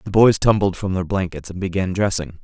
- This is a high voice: No, very low, 95 Hz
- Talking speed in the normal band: No, fast, 220 wpm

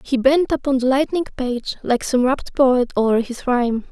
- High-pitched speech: Yes, very high, 255 Hz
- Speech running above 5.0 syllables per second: No, 4.9 syllables/s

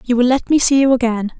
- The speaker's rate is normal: No, fast, 300 wpm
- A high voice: Yes, very high, 250 Hz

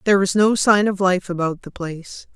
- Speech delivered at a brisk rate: Yes, fast, 230 wpm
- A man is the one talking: No, female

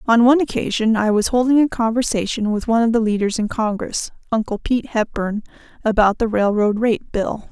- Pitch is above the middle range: Yes, high, 225 Hz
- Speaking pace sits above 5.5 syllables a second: Yes, 5.7 syllables/s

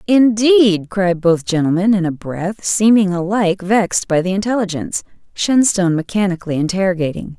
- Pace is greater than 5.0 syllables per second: Yes, 5.3 syllables/s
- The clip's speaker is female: Yes, female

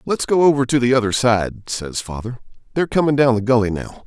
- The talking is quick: Yes, fast, 220 wpm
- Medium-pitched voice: No, low, 125 Hz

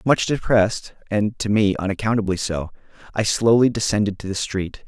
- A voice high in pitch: No, low, 105 Hz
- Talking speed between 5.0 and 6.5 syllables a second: Yes, 5.3 syllables/s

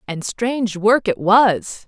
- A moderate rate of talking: Yes, average, 160 wpm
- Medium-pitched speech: No, high, 210 Hz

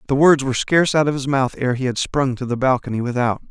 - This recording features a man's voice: Yes, male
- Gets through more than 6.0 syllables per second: Yes, 6.5 syllables/s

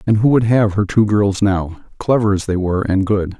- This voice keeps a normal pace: No, fast, 245 wpm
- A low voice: Yes, low, 100 Hz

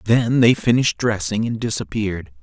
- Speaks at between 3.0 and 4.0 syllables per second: No, 5.4 syllables/s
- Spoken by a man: Yes, male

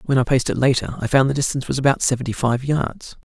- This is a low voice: Yes, low, 130 Hz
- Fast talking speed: Yes, fast, 255 wpm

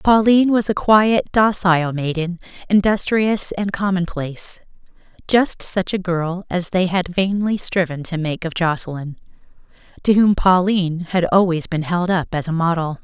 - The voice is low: No, medium, 180 Hz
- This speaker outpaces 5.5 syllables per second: No, 4.6 syllables/s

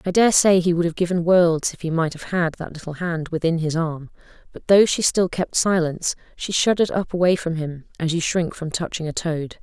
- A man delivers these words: No, female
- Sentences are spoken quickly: Yes, fast, 235 wpm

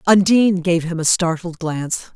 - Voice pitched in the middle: Yes, medium, 175 Hz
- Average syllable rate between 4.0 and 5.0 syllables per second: No, 5.2 syllables/s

